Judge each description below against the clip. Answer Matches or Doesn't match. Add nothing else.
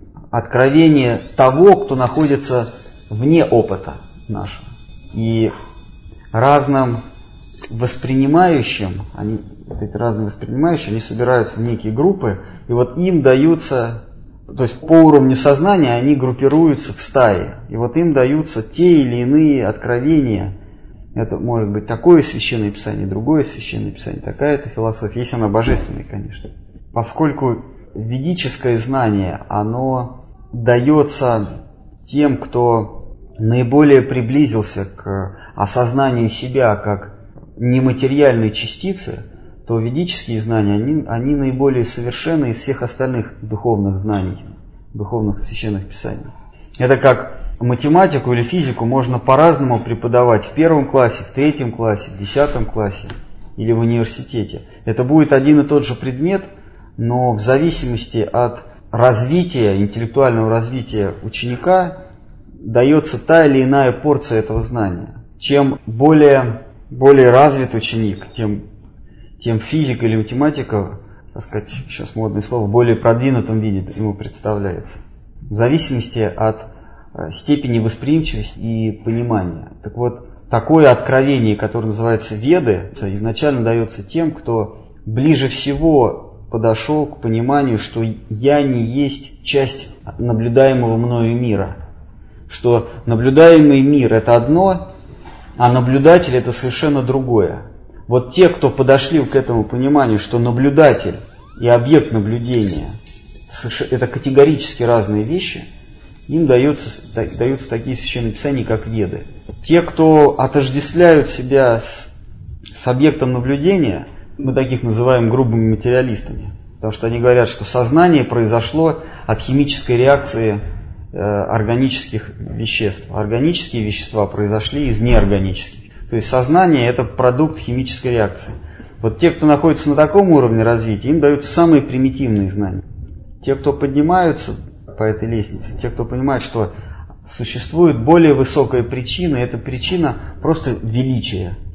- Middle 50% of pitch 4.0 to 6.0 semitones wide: Matches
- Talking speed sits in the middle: Matches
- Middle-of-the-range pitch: Doesn't match